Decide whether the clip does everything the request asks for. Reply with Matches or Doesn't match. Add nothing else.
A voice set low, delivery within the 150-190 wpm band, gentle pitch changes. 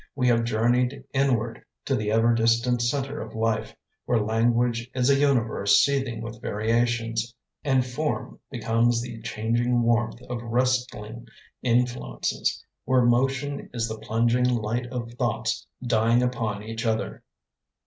Doesn't match